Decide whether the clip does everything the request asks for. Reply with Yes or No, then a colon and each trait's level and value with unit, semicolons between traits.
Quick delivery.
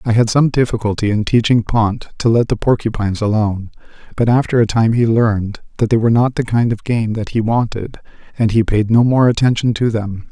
Yes: fast, 215 wpm